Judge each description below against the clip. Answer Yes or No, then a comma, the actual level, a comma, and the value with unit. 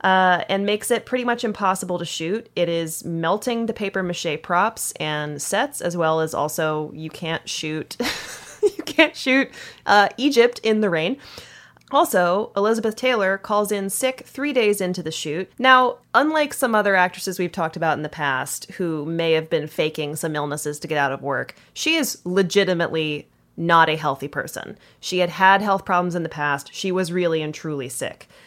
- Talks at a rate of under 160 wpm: No, average, 185 wpm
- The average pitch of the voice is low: No, medium, 180 Hz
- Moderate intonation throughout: Yes, average, 5.0 semitones